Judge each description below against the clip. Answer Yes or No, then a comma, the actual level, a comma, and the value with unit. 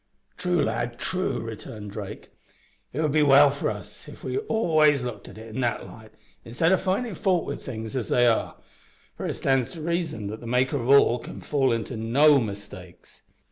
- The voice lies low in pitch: Yes, low, 130 Hz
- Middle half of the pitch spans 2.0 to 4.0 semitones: No, wide, 5.5 semitones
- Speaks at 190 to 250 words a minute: Yes, average, 195 wpm